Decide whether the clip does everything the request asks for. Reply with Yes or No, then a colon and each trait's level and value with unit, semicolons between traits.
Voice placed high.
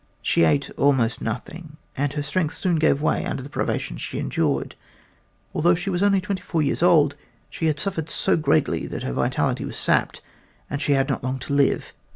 No: medium, 150 Hz